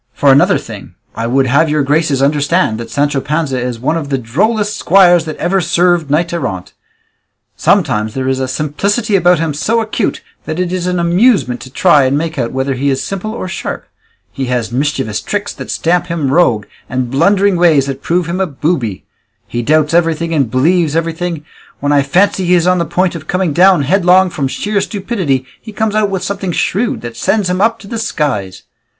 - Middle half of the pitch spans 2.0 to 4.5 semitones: No, average, 5.3 semitones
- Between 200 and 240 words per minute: Yes, fast, 205 wpm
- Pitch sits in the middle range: Yes, medium, 165 Hz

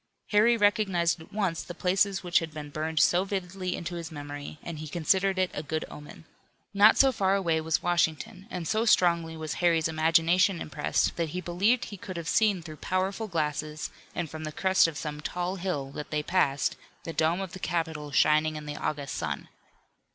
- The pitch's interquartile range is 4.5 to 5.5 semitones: No, average, 3.3 semitones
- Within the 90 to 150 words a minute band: No, average, 195 wpm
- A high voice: No, medium, 170 Hz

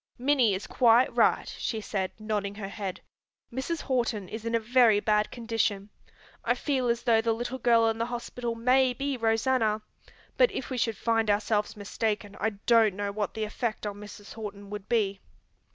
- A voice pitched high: Yes, high, 225 Hz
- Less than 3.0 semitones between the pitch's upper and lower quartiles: Yes, narrow, 2.5 semitones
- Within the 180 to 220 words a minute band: Yes, average, 185 wpm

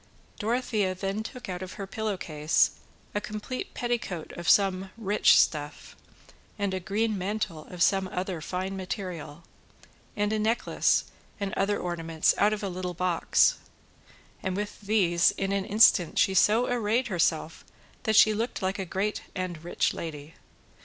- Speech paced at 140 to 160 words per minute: Yes, average, 155 wpm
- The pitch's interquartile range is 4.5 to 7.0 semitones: No, average, 3.0 semitones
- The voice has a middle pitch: No, high, 195 Hz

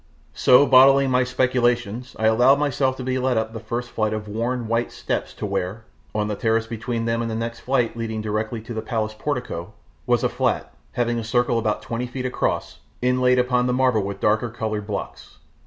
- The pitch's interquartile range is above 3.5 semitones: No, narrow, 2.5 semitones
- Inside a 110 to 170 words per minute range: No, fast, 205 wpm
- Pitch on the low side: Yes, low, 115 Hz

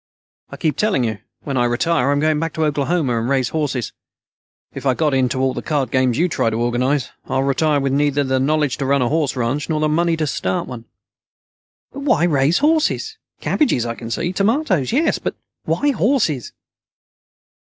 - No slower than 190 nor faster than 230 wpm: Yes, average, 195 wpm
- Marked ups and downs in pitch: No, average, 4.2 semitones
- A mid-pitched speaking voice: Yes, medium, 145 Hz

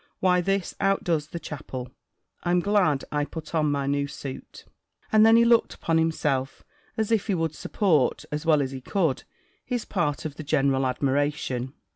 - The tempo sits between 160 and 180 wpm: Yes, average, 175 wpm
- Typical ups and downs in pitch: Yes, average, 4.8 semitones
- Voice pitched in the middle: Yes, medium, 155 Hz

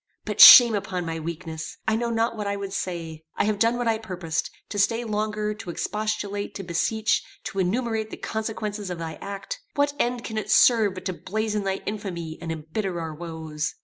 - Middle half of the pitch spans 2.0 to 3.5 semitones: No, average, 4.2 semitones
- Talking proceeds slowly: No, average, 200 wpm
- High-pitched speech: Yes, high, 205 Hz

